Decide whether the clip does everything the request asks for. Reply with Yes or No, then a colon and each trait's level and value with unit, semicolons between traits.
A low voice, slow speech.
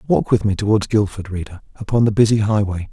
No: low, 105 Hz; fast, 205 wpm